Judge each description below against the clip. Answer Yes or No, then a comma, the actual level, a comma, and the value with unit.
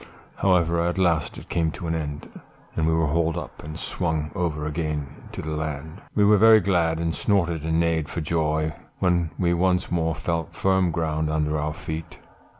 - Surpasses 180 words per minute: Yes, average, 190 wpm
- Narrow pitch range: Yes, narrow, 2.0 semitones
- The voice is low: Yes, very low, 80 Hz